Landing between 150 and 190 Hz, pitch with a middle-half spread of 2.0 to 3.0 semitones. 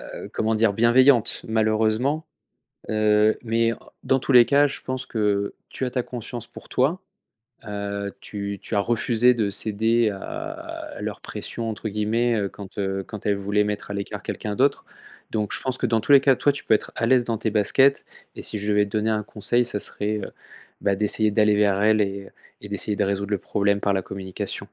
No: low, 110 Hz; average, 2.7 semitones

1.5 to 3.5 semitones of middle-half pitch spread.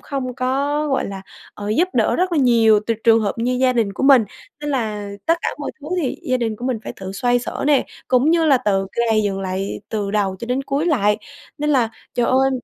No: average, 4.6 semitones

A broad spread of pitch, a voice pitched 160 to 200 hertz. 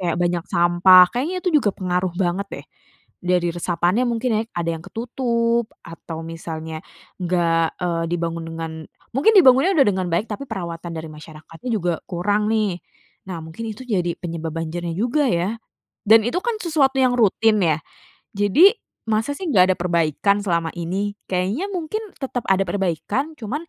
Yes: wide, 5.7 semitones; medium, 185 Hz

